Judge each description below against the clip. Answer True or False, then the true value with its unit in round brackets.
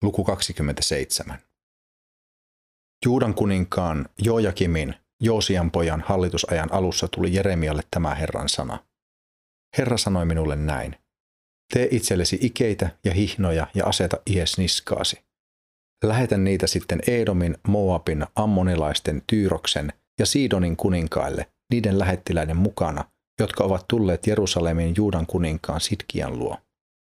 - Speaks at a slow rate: False (105 wpm)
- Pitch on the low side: True (90 Hz)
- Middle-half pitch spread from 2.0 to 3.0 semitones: False (4.2 semitones)